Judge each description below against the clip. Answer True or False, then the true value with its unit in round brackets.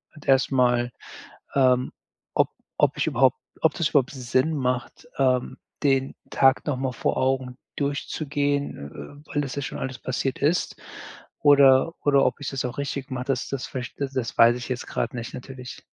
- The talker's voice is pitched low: True (130 Hz)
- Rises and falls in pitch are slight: True (2.0 semitones)